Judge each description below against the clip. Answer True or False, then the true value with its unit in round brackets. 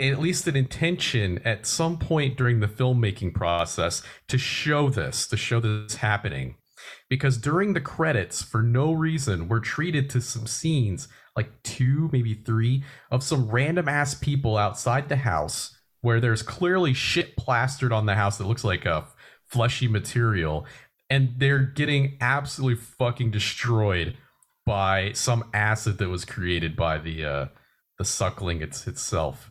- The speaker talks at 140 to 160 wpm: True (155 wpm)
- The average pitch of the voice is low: True (120 Hz)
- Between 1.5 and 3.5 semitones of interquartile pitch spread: False (4.6 semitones)